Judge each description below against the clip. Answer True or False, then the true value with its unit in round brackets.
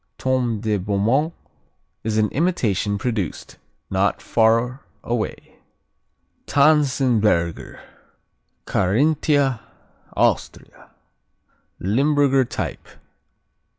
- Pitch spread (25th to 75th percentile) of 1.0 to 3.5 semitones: False (5.0 semitones)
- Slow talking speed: True (65 wpm)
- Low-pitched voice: True (120 Hz)